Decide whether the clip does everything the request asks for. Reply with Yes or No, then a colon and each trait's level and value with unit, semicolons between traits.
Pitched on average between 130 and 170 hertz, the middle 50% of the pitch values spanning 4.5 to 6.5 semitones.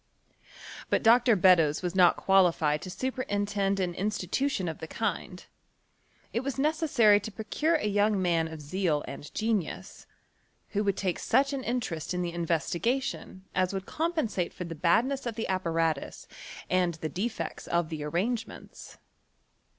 No: high, 190 Hz; average, 5.2 semitones